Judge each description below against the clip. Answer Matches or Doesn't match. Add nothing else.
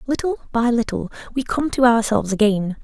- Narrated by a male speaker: Doesn't match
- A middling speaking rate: Matches